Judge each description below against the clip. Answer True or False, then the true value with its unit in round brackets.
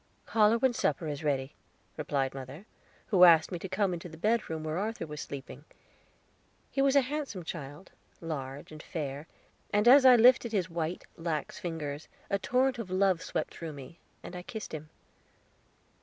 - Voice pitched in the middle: True (170 Hz)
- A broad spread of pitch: True (6.0 semitones)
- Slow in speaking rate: False (175 wpm)